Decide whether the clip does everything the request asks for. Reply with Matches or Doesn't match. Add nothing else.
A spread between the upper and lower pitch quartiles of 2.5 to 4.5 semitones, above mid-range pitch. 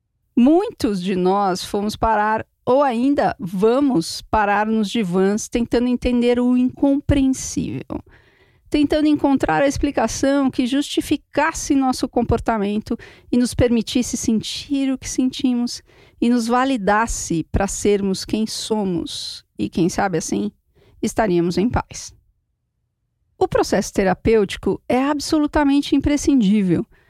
Doesn't match